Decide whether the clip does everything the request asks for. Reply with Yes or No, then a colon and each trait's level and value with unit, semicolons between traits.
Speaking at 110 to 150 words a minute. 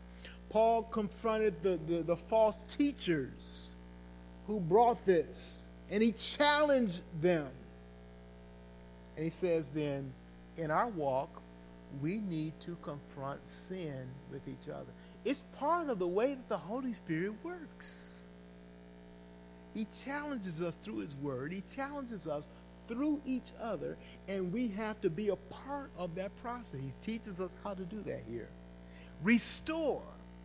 Yes: average, 140 wpm